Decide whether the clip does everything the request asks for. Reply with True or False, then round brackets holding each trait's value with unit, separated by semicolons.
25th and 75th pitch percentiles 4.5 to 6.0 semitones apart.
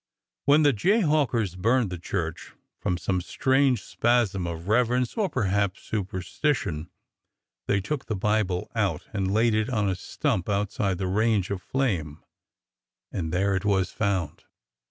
True (4.8 semitones)